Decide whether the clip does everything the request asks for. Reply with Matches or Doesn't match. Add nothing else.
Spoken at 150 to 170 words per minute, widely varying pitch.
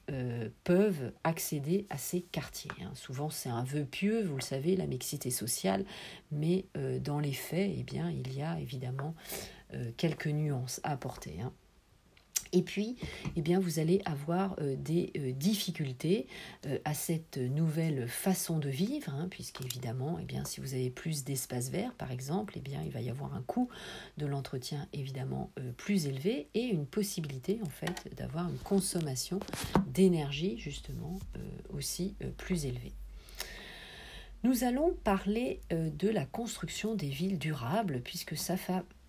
Matches